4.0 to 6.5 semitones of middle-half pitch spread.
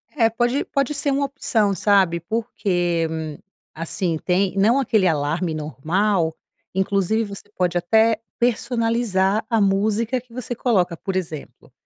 Yes: average, 4.5 semitones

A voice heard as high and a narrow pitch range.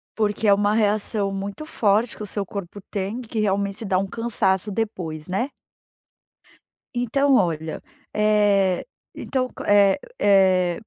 Yes: high, 205 Hz; narrow, 2.2 semitones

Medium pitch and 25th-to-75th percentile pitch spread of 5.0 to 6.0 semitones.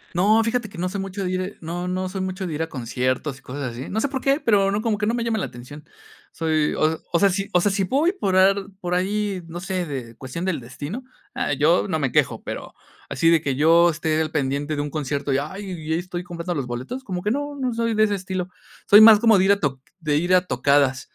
Yes: medium, 180 Hz; average, 5.3 semitones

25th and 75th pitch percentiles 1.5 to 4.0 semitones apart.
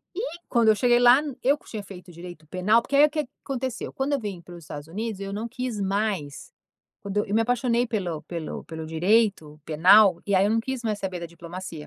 No: wide, 5.5 semitones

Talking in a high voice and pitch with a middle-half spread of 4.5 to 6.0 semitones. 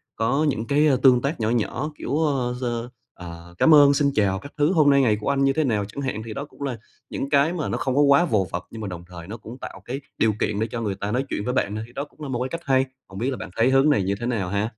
No: low, 125 Hz; average, 4.8 semitones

